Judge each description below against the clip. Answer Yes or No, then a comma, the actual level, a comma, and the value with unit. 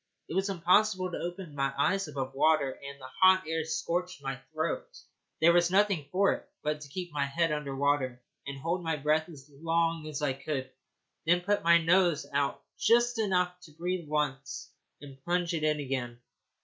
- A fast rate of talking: No, average, 190 wpm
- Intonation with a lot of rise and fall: No, average, 4.1 semitones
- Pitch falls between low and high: Yes, medium, 160 Hz